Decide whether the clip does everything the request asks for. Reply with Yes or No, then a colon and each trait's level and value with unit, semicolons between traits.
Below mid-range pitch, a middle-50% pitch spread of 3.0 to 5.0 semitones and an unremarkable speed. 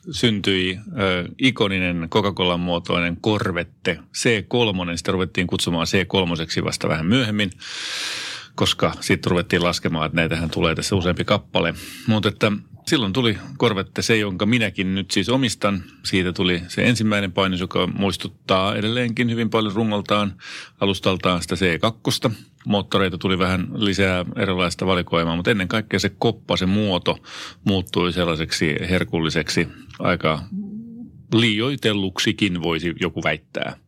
Yes: very low, 95 Hz; average, 3.4 semitones; average, 125 wpm